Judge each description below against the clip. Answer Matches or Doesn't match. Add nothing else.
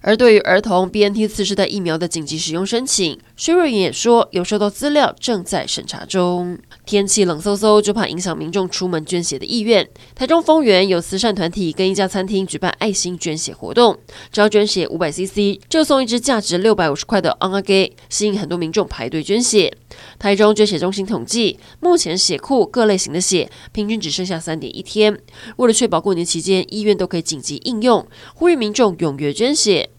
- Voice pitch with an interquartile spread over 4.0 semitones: Doesn't match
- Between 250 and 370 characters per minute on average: Matches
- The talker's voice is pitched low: Doesn't match